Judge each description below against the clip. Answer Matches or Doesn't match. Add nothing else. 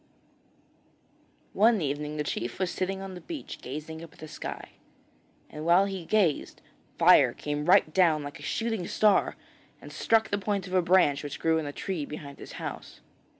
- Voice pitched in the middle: Matches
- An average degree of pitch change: Matches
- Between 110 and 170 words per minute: Doesn't match